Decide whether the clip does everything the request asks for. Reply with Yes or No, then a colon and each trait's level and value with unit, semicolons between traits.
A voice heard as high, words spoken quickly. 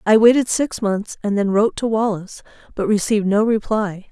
No: high, 210 Hz; average, 190 wpm